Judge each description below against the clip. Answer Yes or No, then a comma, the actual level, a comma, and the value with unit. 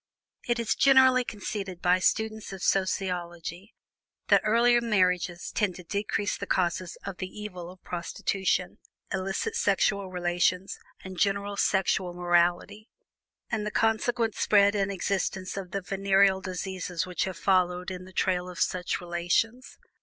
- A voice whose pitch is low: No, high, 190 Hz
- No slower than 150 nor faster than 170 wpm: No, average, 140 wpm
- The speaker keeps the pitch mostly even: Yes, narrow, 2.3 semitones